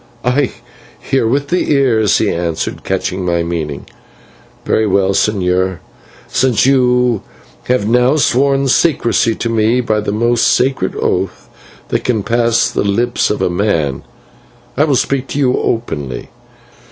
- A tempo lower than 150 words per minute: Yes, average, 140 wpm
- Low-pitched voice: Yes, low, 115 Hz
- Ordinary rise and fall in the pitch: Yes, average, 5.0 semitones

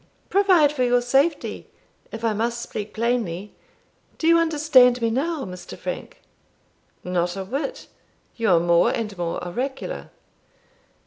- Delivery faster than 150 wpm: No, slow, 135 wpm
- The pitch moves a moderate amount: No, wide, 6.7 semitones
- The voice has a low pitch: No, high, 240 Hz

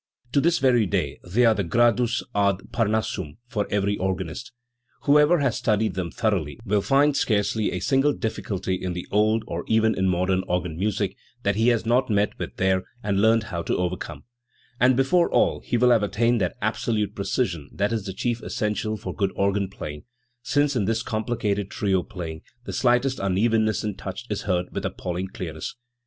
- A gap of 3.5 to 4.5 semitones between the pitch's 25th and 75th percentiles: Yes, average, 3.8 semitones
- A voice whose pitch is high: No, low, 105 Hz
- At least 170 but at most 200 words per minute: Yes, average, 185 wpm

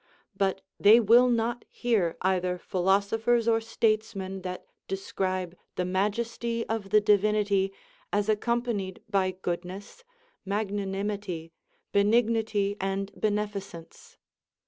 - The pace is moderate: No, slow, 100 wpm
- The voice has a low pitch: No, high, 200 Hz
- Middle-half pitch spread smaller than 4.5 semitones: Yes, average, 2.7 semitones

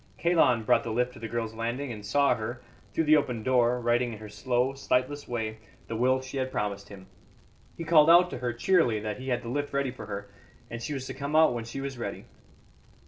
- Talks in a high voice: No, low, 125 Hz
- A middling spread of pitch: Yes, average, 3.4 semitones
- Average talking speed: No, fast, 235 wpm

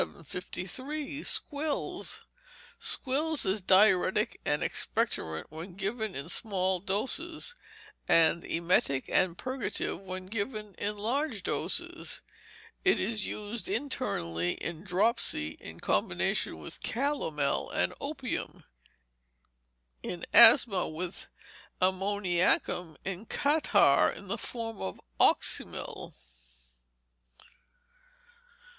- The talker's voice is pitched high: Yes, high, 195 Hz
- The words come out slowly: Yes, slow, 90 wpm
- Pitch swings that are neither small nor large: No, wide, 5.9 semitones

